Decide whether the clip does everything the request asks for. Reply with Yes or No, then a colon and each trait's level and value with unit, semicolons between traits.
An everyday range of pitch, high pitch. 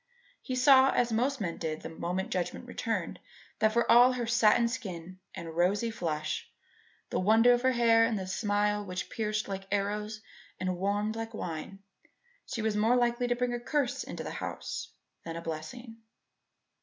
Yes: average, 4.2 semitones; high, 215 Hz